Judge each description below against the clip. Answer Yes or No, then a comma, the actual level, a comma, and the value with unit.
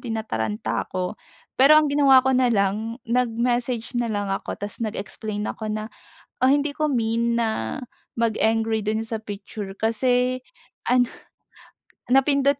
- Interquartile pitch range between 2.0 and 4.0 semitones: Yes, average, 2.9 semitones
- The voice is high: Yes, high, 225 Hz